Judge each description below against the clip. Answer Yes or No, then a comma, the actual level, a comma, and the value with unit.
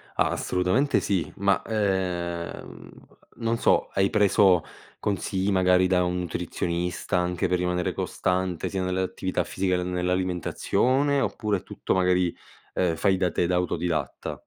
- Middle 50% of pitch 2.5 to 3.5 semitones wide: No, narrow, 1.6 semitones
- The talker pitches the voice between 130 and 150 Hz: No, very low, 90 Hz